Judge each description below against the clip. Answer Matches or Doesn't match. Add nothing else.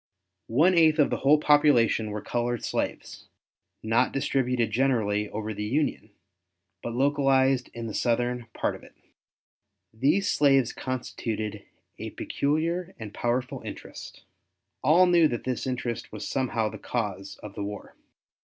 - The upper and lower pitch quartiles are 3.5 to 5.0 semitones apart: Matches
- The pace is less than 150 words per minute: Matches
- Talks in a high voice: Doesn't match